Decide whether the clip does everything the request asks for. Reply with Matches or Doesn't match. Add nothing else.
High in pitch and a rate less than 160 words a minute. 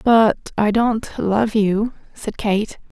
Matches